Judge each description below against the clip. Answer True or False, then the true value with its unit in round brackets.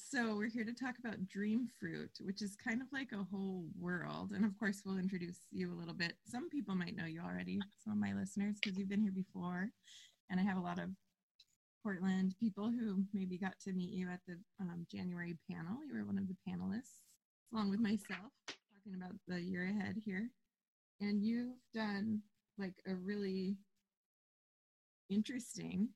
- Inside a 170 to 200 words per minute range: True (185 wpm)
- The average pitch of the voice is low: False (200 Hz)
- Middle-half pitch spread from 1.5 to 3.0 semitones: True (2.4 semitones)